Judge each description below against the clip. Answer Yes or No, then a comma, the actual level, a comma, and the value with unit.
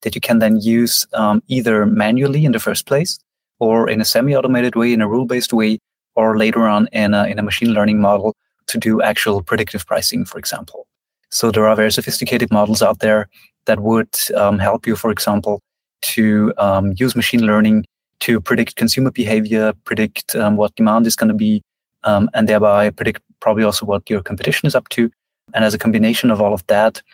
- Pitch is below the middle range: Yes, low, 110 Hz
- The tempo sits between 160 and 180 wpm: No, fast, 205 wpm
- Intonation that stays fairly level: Yes, narrow, 1.7 semitones